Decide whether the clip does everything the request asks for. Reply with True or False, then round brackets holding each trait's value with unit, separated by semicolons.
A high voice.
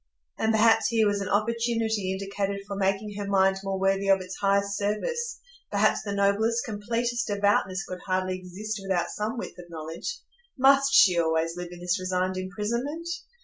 True (200 Hz)